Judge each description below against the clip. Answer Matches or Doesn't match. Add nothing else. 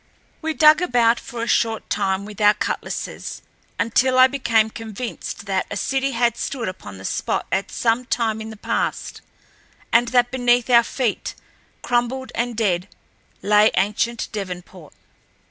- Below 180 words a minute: Matches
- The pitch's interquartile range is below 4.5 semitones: Matches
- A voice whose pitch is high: Matches